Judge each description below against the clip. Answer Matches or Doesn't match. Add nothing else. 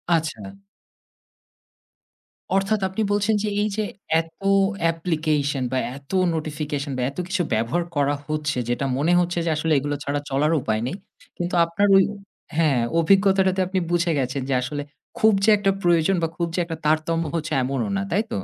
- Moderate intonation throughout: Matches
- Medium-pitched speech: Matches